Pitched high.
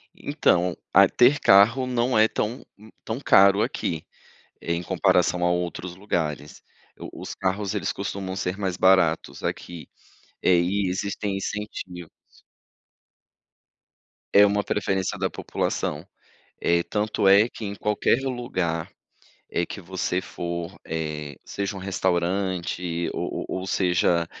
No: very low, 95 Hz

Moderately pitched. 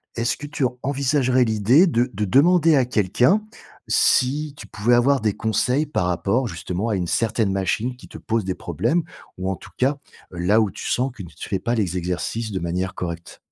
No: low, 115 Hz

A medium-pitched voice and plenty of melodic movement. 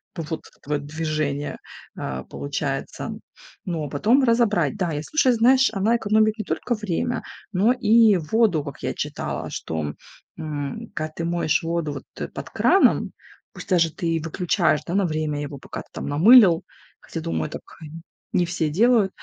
Yes: medium, 170 Hz; wide, 6.2 semitones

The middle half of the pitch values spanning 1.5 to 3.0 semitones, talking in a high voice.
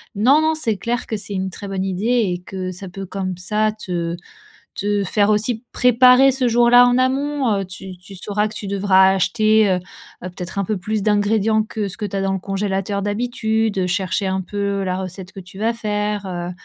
Yes: average, 2.7 semitones; high, 205 Hz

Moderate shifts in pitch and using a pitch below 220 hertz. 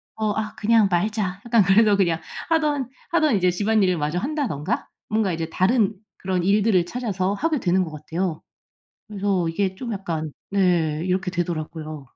Yes: average, 3.9 semitones; high, 190 Hz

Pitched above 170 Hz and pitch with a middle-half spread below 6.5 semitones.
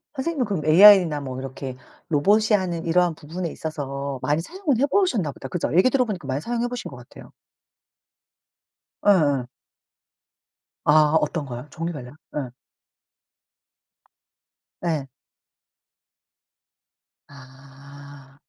No: medium, 155 Hz; wide, 5.8 semitones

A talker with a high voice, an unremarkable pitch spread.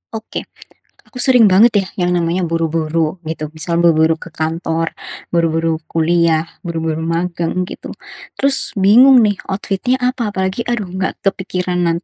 No: medium, 175 Hz; average, 3.2 semitones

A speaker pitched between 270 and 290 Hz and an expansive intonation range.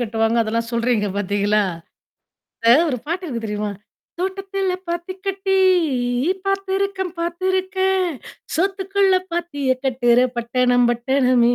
Yes: very high, 285 Hz; wide, 8.2 semitones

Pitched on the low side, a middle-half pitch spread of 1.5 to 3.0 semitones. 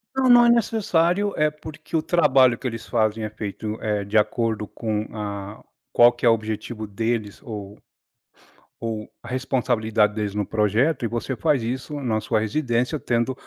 No: low, 115 Hz; average, 3.9 semitones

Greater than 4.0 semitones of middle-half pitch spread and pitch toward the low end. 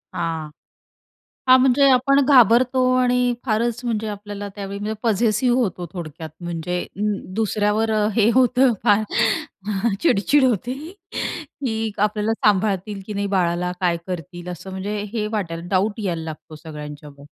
No: average, 4.7 semitones; high, 205 Hz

